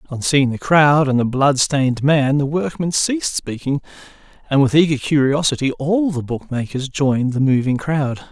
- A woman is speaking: No, male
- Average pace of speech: Yes, average, 165 wpm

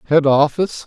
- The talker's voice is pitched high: No, medium, 145 Hz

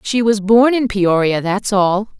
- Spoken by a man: No, female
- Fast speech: No, average, 190 wpm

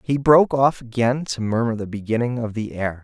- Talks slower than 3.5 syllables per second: No, 5.5 syllables/s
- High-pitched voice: No, low, 120 Hz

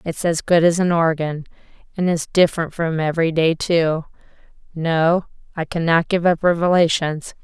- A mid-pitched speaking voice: Yes, medium, 165 Hz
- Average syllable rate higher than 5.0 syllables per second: No, 4.8 syllables/s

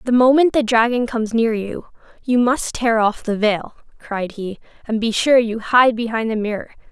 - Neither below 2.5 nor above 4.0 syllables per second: No, 4.8 syllables/s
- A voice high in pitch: Yes, high, 230 Hz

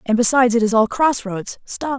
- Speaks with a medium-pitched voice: No, high, 235 Hz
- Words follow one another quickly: Yes, fast, 240 wpm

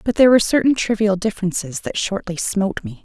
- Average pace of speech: Yes, average, 195 wpm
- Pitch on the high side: Yes, high, 200 Hz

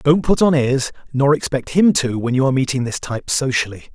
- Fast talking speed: Yes, fast, 230 wpm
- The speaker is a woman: No, male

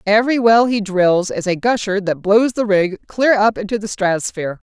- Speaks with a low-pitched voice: No, high, 205 Hz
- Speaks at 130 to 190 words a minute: No, fast, 205 wpm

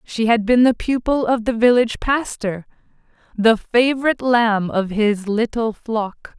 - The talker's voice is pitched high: Yes, high, 230 Hz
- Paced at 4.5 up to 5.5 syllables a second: No, 4.3 syllables/s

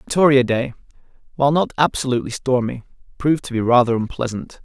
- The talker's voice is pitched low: Yes, low, 130 Hz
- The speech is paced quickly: No, average, 140 wpm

